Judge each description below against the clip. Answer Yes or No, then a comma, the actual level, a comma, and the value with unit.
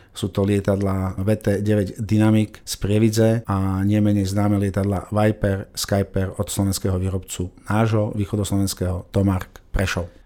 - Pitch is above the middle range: No, low, 100 Hz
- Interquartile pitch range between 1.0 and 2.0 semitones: Yes, narrow, 1.7 semitones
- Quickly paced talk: No, average, 115 wpm